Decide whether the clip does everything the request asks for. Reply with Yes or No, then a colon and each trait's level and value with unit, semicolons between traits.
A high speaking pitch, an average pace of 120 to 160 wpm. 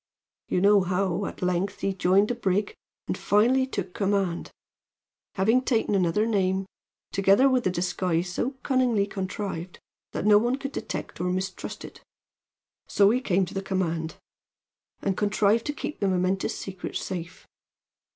Yes: high, 195 Hz; average, 155 wpm